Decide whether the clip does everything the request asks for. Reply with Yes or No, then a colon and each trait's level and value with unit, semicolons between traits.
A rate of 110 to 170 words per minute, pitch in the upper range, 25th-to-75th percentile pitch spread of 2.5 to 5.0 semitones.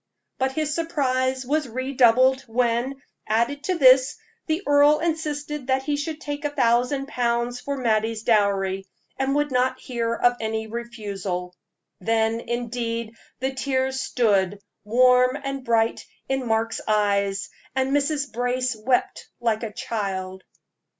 Yes: slow, 135 wpm; very high, 250 Hz; average, 3.4 semitones